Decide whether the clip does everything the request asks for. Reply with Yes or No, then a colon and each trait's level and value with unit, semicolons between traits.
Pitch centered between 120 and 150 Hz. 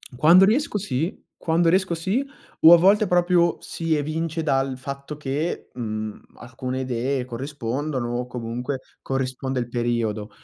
Yes: medium, 140 Hz